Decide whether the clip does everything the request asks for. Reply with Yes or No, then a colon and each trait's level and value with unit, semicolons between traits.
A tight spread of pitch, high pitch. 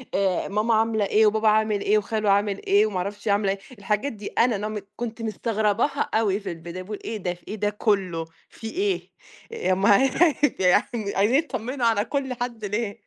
Yes: narrow, 2.2 semitones; high, 210 Hz